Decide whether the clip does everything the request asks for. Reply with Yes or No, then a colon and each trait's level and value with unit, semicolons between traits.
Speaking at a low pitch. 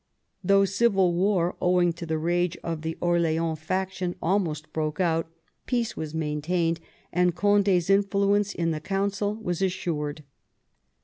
No: medium, 175 Hz